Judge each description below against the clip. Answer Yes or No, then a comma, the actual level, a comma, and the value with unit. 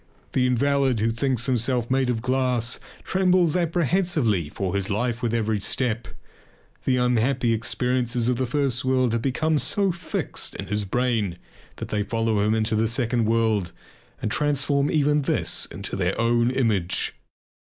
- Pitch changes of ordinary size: Yes, average, 3.1 semitones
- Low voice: Yes, low, 120 Hz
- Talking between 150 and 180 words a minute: Yes, average, 155 wpm